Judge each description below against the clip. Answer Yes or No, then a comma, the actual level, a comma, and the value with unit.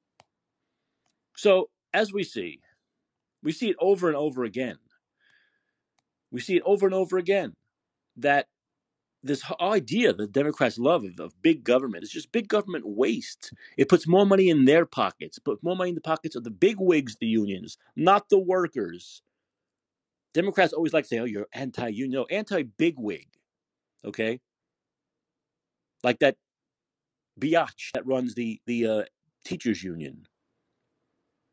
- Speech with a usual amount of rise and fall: No, wide, 7.6 semitones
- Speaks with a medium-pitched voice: Yes, medium, 155 Hz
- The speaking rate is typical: Yes, average, 150 wpm